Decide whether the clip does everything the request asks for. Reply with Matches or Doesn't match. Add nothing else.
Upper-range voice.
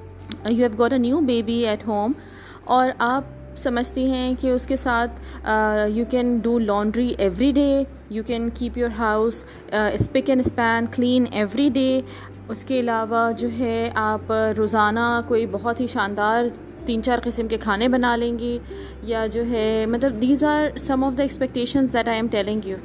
Matches